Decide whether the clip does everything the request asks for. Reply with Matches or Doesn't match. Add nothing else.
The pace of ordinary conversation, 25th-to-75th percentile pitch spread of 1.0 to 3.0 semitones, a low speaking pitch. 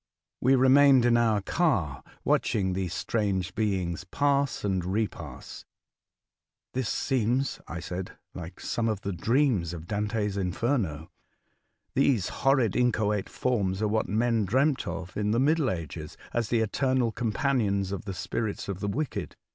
Doesn't match